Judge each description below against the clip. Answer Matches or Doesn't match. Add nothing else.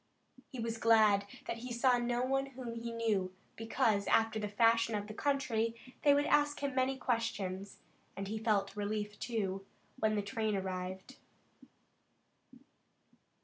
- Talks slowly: Doesn't match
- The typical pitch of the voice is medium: Doesn't match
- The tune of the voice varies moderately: Matches